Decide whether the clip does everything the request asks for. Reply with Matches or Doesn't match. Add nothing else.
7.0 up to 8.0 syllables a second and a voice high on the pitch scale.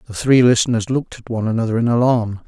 Doesn't match